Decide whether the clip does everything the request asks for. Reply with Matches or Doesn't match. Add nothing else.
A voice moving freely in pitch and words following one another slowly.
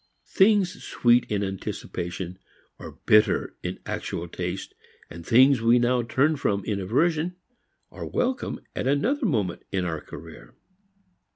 Matches